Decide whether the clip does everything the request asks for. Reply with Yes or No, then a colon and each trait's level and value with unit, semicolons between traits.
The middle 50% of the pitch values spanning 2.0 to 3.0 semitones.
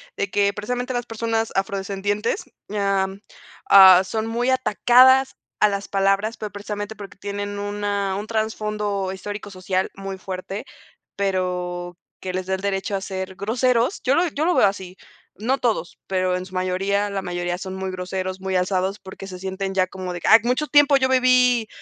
Yes: average, 2.7 semitones